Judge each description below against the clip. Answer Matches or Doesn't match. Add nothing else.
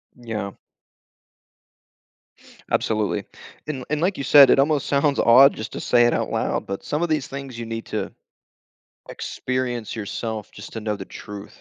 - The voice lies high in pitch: Doesn't match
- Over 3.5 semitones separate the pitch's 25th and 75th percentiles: Matches